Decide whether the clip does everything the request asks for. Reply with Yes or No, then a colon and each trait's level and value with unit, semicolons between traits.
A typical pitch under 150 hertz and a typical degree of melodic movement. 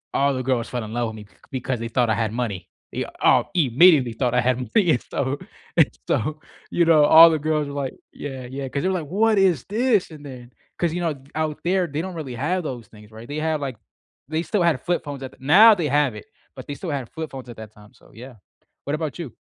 Yes: medium, 140 Hz; average, 5.0 semitones